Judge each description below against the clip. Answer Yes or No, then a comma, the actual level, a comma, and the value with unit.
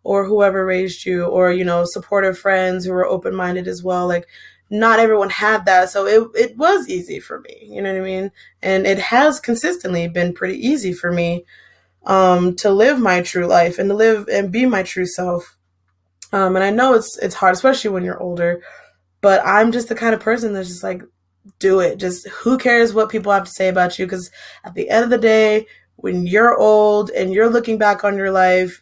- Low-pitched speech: No, high, 195 Hz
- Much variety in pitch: No, average, 3.4 semitones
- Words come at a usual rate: No, fast, 220 wpm